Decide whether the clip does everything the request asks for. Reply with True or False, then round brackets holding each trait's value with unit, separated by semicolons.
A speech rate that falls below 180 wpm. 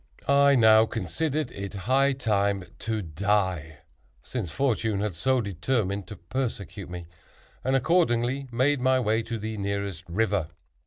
True (140 wpm)